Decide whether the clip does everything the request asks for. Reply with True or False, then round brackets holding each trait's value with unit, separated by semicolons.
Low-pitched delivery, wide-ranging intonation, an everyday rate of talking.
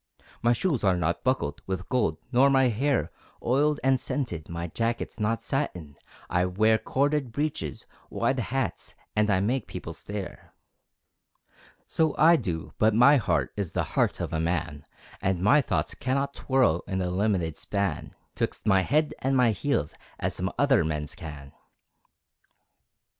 True (110 Hz; 7.1 semitones; 155 wpm)